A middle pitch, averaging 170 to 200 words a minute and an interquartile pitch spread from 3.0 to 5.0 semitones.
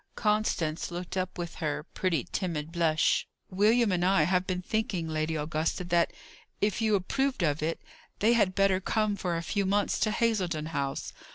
Yes: medium, 180 Hz; average, 175 wpm; average, 4.0 semitones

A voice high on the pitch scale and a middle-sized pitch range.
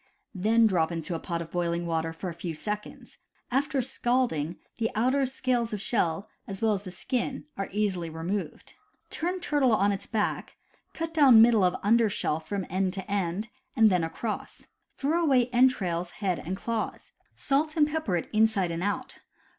No: high, 210 Hz; wide, 5.8 semitones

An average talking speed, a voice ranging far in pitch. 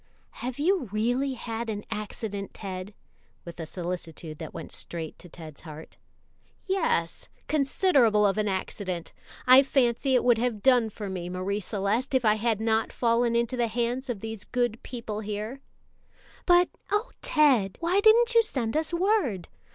No: average, 160 wpm; average, 4.8 semitones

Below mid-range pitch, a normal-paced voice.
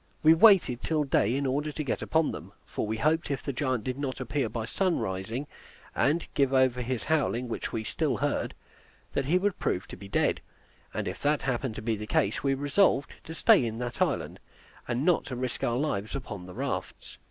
No: low, 130 Hz; fast, 210 wpm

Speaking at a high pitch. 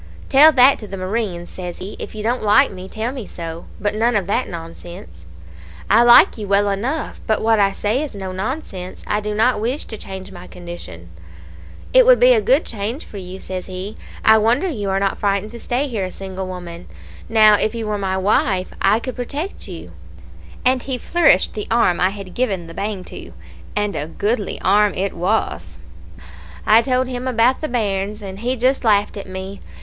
Yes: high, 210 Hz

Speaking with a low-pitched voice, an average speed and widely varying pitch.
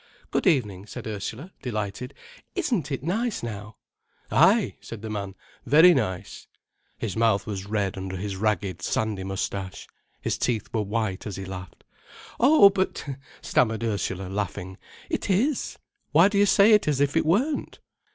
Yes: low, 110 Hz; average, 155 wpm; wide, 8.7 semitones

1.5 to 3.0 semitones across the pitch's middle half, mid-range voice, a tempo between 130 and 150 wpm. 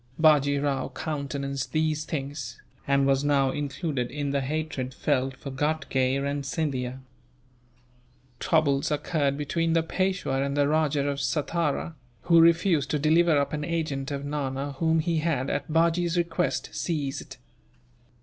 Yes: narrow, 2.5 semitones; medium, 145 Hz; average, 140 wpm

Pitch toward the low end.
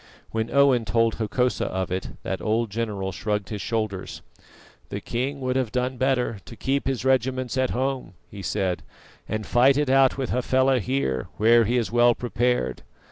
Yes: low, 120 Hz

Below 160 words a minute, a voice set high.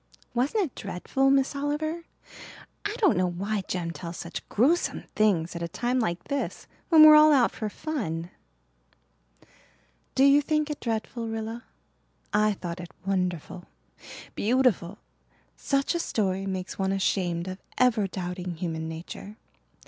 Yes: average, 140 wpm; high, 210 Hz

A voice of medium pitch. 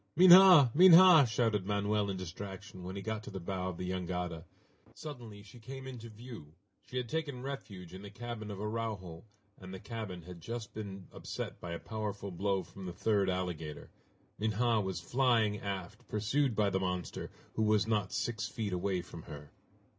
No: low, 105 Hz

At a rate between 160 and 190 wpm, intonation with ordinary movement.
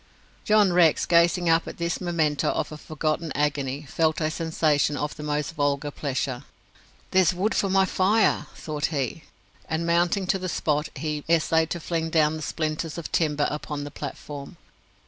No: average, 170 wpm; narrow, 2.3 semitones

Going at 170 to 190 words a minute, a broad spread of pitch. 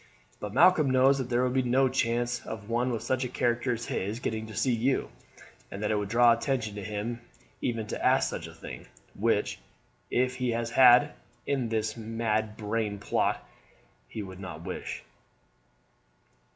No: average, 180 wpm; average, 2.8 semitones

